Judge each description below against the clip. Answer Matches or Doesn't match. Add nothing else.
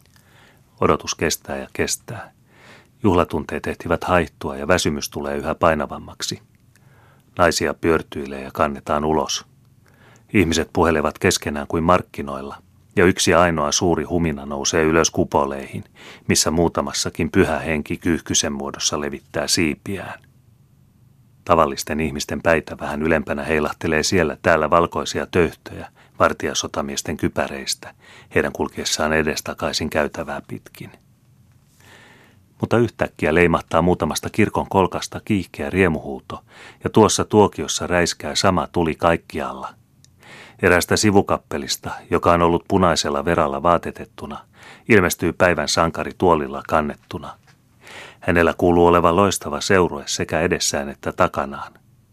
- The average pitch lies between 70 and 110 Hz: Matches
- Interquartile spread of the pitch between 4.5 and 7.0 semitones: Matches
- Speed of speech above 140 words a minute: Doesn't match